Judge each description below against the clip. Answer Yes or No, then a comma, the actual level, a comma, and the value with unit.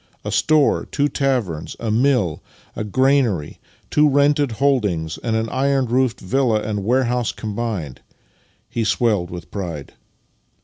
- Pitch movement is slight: No, average, 4.9 semitones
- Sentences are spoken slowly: Yes, slow, 130 wpm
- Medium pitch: No, low, 115 Hz